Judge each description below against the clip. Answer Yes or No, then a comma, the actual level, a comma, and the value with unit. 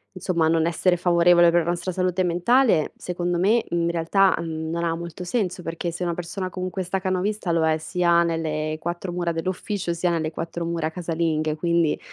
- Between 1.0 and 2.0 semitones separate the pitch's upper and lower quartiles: Yes, narrow, 1.7 semitones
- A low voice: No, medium, 170 Hz